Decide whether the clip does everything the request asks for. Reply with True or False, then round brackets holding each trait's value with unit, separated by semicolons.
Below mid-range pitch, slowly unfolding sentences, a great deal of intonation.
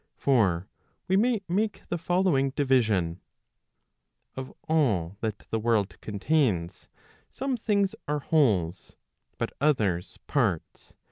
True (130 Hz; 110 wpm; 8.4 semitones)